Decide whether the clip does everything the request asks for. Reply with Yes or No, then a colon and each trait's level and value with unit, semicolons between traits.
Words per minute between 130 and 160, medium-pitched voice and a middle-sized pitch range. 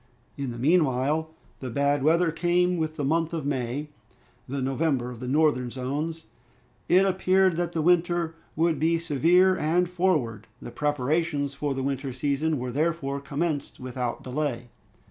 Yes: average, 155 wpm; medium, 150 Hz; average, 3.9 semitones